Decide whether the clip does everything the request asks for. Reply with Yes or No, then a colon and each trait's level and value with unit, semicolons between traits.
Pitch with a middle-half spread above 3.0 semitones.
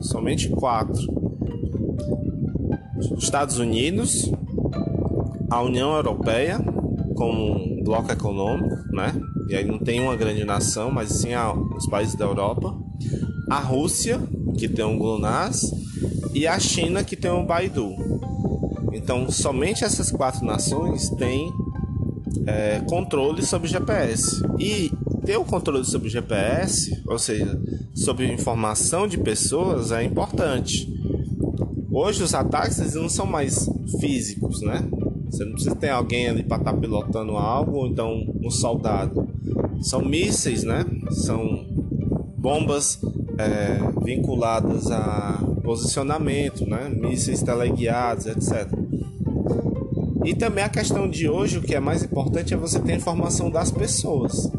No: narrow, 2.5 semitones